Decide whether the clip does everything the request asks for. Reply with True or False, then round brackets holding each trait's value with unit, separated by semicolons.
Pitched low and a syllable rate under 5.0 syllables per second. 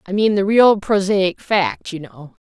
False (190 Hz; 4.0 syllables/s)